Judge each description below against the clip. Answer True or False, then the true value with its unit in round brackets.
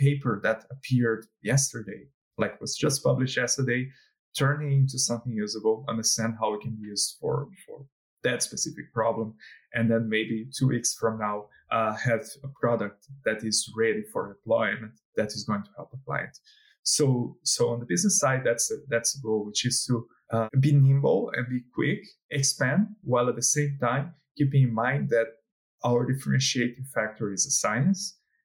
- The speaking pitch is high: False (125 Hz)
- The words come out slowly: False (175 wpm)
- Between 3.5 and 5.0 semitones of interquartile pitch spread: True (3.8 semitones)